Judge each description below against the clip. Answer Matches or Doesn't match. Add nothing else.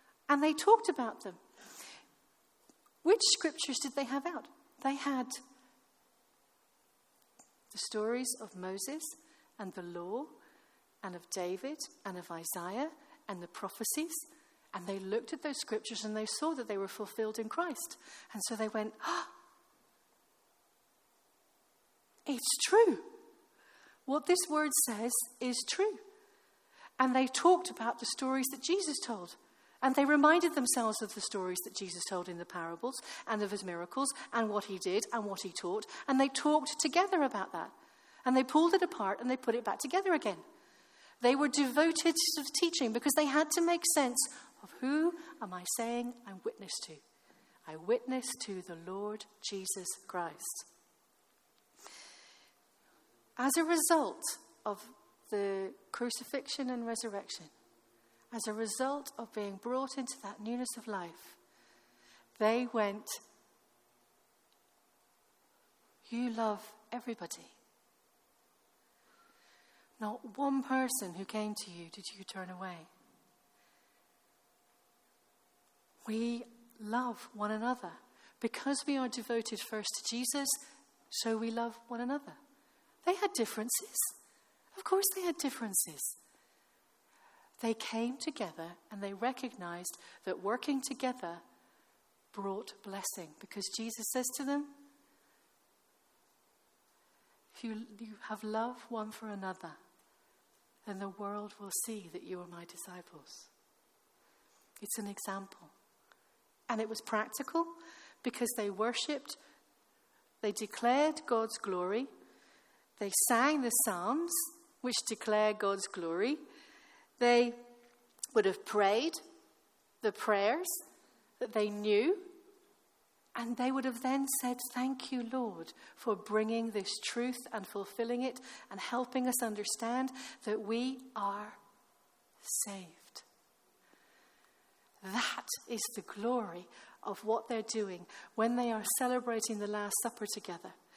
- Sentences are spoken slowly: Matches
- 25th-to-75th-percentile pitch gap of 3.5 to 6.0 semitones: Matches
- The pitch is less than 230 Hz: Doesn't match